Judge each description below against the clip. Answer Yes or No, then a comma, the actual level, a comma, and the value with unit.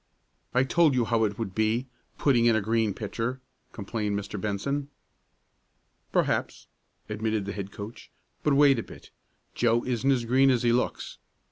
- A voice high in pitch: No, low, 115 Hz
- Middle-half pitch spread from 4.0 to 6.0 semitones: No, average, 3.3 semitones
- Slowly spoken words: No, average, 160 wpm